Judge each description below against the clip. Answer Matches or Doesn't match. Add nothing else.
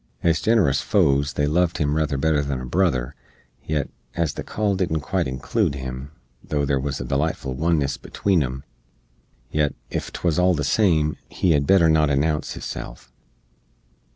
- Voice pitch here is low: Matches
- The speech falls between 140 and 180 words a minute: Matches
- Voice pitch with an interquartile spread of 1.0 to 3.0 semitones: Doesn't match